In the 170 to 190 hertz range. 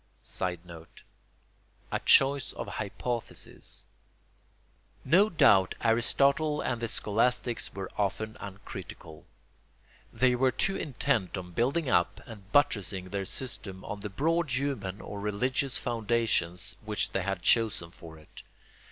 No: low, 110 Hz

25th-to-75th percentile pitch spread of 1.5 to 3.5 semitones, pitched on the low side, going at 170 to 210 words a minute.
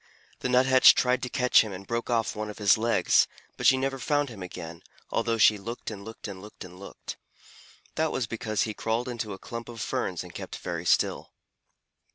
Yes: average, 3.2 semitones; low, 115 Hz; fast, 205 wpm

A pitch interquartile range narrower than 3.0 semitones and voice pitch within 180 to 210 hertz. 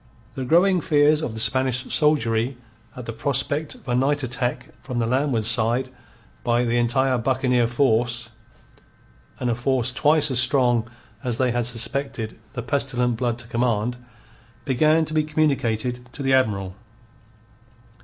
No: narrow, 2.6 semitones; low, 125 Hz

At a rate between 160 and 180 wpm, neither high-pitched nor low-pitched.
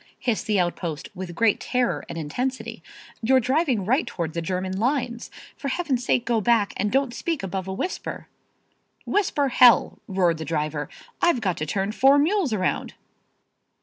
No: average, 165 wpm; high, 225 Hz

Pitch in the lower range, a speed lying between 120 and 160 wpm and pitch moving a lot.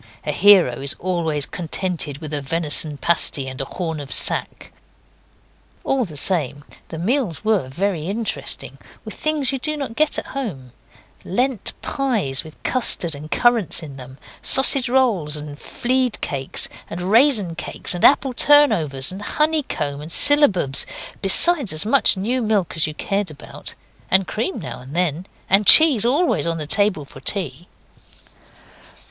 No: medium, 185 Hz; average, 155 wpm; wide, 8.3 semitones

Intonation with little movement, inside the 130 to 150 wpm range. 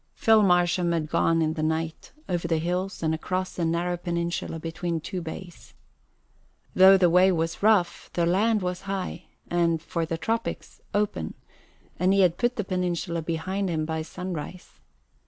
No: narrow, 2.1 semitones; average, 165 wpm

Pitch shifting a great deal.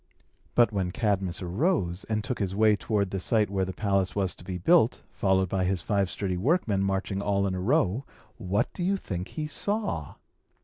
No: average, 3.1 semitones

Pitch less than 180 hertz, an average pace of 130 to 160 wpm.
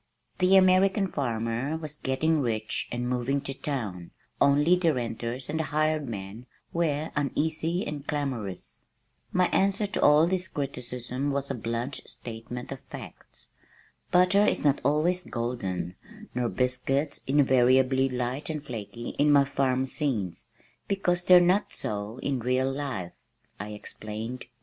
Yes: low, 135 Hz; average, 140 wpm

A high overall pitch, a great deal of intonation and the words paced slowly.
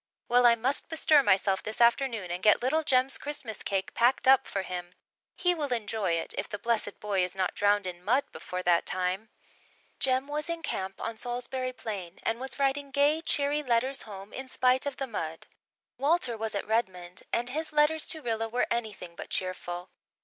No: high, 235 Hz; wide, 5.9 semitones; average, 195 wpm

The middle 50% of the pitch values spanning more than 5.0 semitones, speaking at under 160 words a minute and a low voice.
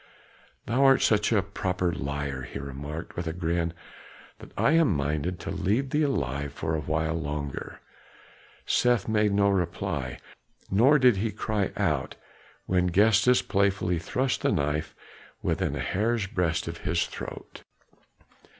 Yes: wide, 5.5 semitones; average, 145 wpm; very low, 90 Hz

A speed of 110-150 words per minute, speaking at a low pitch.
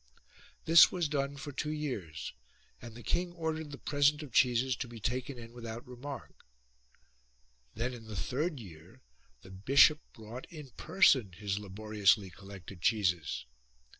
Yes: average, 145 wpm; low, 120 Hz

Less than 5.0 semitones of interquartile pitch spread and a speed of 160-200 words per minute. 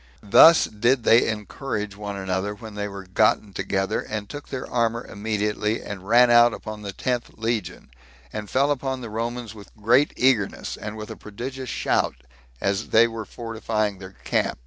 Yes: narrow, 2.6 semitones; average, 170 wpm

